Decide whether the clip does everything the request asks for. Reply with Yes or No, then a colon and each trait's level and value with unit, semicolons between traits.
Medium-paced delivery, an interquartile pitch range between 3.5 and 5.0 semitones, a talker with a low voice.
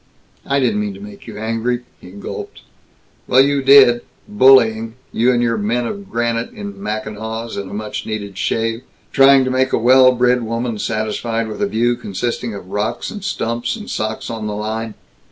No: average, 185 wpm; average, 3.1 semitones; low, 115 Hz